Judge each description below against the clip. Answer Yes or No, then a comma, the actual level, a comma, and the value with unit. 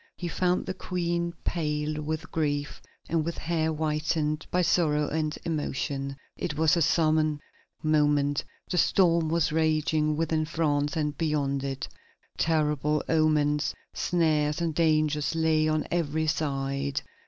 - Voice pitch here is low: No, medium, 155 Hz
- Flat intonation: Yes, narrow, 1.6 semitones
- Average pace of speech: No, slow, 130 wpm